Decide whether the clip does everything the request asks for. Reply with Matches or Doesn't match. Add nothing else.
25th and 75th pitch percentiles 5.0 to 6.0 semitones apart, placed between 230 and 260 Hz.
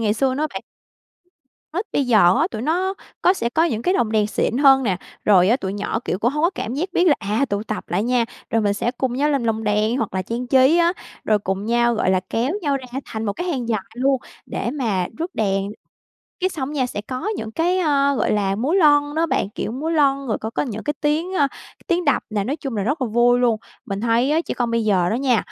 Matches